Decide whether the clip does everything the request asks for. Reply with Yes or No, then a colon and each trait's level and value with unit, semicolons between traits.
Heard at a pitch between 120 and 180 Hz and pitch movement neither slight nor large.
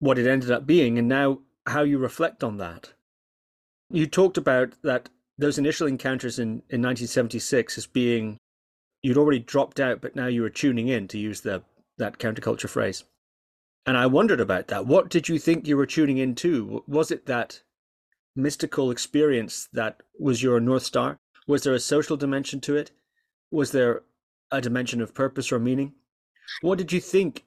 Yes: low, 135 Hz; average, 3.5 semitones